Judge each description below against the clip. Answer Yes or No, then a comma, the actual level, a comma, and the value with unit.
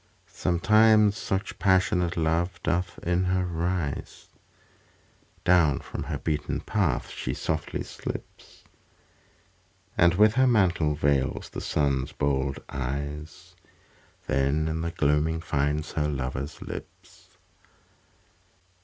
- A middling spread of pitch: Yes, average, 3.8 semitones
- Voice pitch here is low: Yes, very low, 80 Hz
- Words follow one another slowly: Yes, slow, 105 wpm